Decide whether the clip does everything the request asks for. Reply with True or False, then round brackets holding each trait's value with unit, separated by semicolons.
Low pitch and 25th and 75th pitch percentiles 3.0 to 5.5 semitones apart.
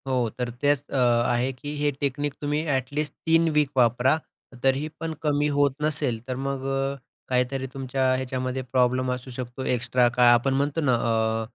False (130 Hz; 2.5 semitones)